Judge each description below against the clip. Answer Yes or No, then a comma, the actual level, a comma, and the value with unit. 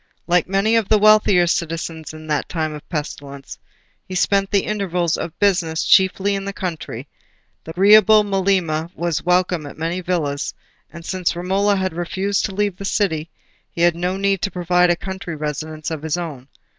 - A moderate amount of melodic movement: Yes, average, 3.4 semitones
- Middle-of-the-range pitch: Yes, medium, 180 Hz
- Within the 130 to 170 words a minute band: No, average, 180 wpm